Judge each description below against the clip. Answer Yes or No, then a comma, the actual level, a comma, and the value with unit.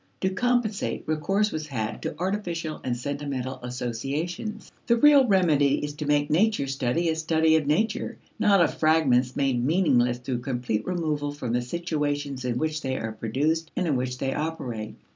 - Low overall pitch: No, medium, 150 Hz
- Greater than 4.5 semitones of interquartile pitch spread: Yes, average, 4.9 semitones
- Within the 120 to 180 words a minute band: Yes, average, 170 wpm